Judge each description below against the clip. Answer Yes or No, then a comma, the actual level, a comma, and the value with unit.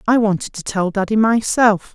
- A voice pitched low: No, high, 210 Hz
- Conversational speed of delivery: Yes, average, 185 wpm